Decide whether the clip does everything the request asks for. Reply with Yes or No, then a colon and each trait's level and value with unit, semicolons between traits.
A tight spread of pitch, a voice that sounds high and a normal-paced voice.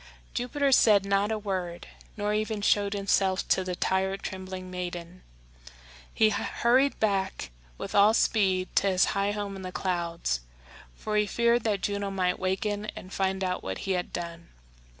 Yes: narrow, 2.2 semitones; high, 195 Hz; average, 165 wpm